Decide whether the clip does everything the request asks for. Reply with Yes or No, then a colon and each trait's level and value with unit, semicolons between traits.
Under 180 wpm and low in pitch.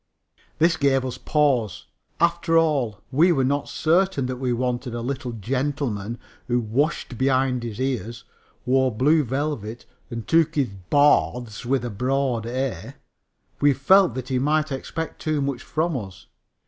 Yes: average, 150 wpm; low, 130 Hz